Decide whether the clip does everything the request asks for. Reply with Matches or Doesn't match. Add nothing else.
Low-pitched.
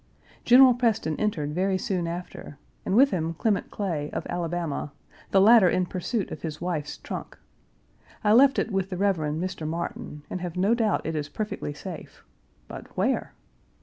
Doesn't match